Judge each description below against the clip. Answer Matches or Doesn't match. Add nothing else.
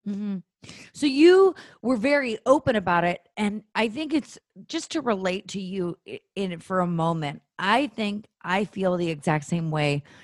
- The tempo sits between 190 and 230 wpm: Doesn't match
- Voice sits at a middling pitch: Doesn't match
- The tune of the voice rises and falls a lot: Matches